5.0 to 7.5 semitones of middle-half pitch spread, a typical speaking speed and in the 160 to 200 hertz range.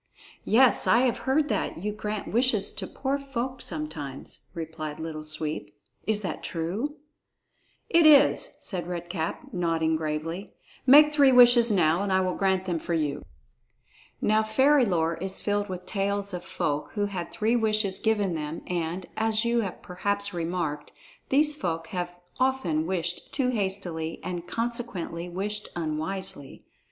Yes: wide, 5.4 semitones; average, 150 wpm; high, 190 Hz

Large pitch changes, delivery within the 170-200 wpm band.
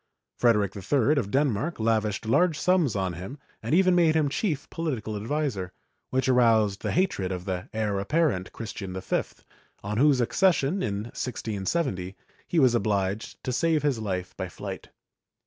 No: wide, 6.9 semitones; average, 155 wpm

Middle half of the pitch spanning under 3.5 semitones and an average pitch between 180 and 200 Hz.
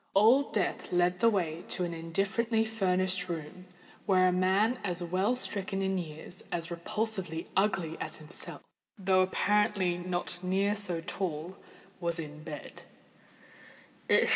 Yes: average, 2.7 semitones; medium, 185 Hz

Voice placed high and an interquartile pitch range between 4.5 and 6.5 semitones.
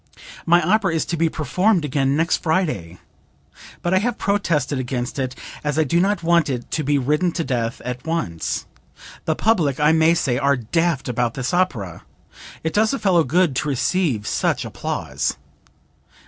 No: medium, 155 Hz; average, 5.1 semitones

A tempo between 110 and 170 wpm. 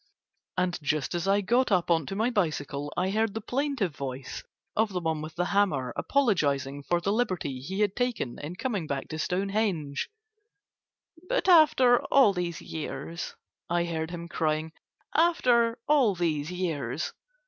Yes: average, 160 wpm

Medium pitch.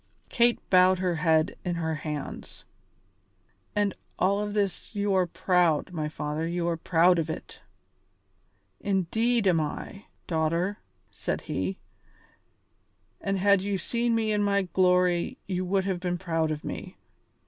Yes: medium, 180 Hz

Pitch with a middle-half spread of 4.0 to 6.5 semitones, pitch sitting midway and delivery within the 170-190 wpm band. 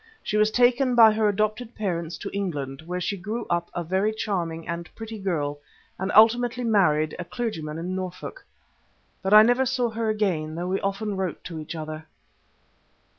No: average, 4.6 semitones; high, 195 Hz; average, 175 wpm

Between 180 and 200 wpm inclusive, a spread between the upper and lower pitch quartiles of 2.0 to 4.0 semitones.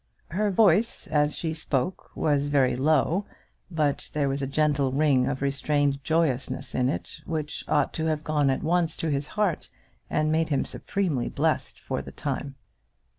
No: average, 170 wpm; narrow, 2.5 semitones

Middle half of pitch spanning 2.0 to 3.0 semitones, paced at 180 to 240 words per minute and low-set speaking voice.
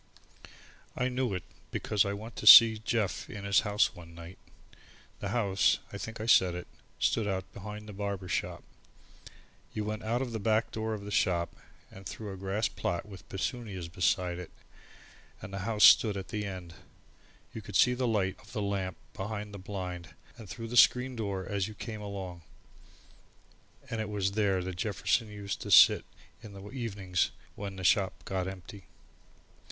Yes: narrow, 2.6 semitones; average, 185 wpm; low, 100 Hz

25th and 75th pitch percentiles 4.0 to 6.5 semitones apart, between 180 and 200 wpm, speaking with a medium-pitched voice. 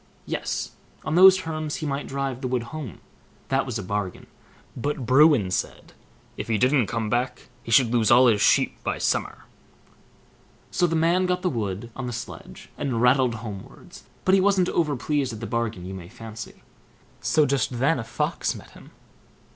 No: average, 5.1 semitones; average, 185 wpm; low, 130 Hz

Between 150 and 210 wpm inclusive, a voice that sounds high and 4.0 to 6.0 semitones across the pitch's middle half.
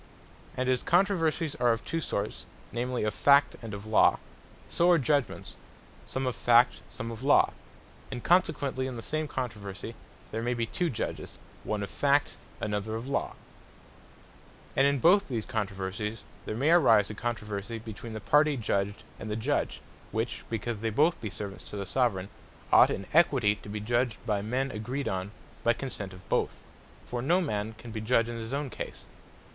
No: average, 180 wpm; low, 115 Hz; average, 4.4 semitones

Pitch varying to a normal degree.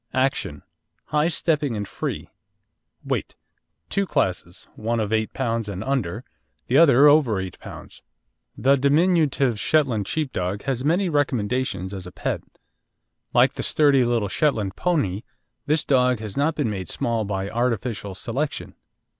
No: wide, 6.0 semitones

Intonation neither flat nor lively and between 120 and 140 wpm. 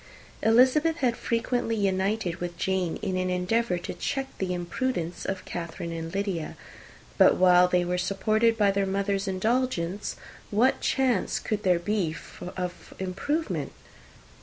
Yes: average, 4.2 semitones; slow, 135 wpm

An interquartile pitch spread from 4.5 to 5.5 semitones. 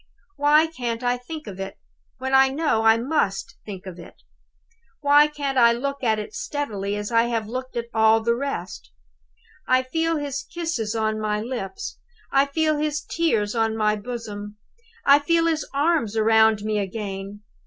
Yes: average, 5.1 semitones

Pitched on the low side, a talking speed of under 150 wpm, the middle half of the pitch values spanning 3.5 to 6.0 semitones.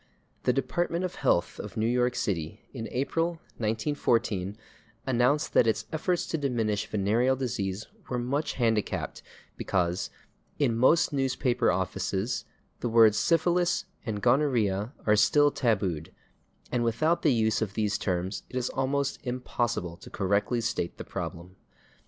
Yes: low, 120 Hz; average, 140 wpm; average, 4.5 semitones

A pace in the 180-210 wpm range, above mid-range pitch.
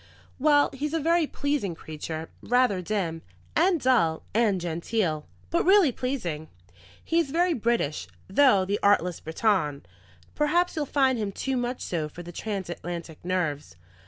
No: average, 145 wpm; high, 210 Hz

